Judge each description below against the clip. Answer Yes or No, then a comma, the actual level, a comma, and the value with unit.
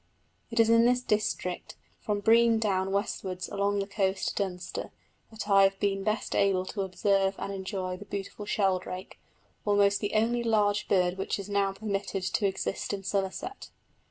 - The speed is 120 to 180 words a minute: Yes, average, 170 wpm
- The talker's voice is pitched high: Yes, high, 200 Hz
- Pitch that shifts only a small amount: Yes, narrow, 1.6 semitones